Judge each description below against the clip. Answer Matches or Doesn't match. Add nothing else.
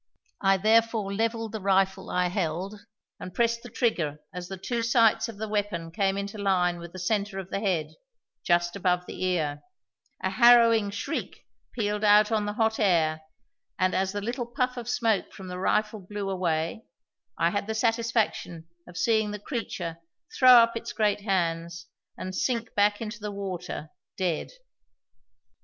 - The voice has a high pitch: Matches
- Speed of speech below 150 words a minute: Doesn't match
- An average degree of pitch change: Matches